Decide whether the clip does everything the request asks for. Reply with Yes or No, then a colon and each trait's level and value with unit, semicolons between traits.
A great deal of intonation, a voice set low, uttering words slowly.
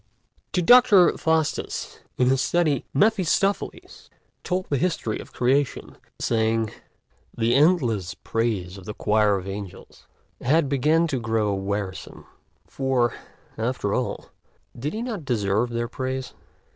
Yes: wide, 6.7 semitones; low, 125 Hz; slow, 130 wpm